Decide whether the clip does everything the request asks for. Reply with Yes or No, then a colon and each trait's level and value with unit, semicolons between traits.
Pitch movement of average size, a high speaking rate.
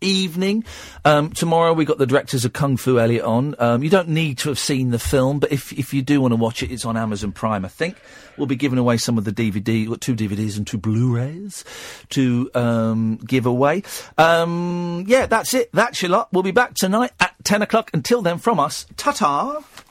No: wide, 7.3 semitones; fast, 220 wpm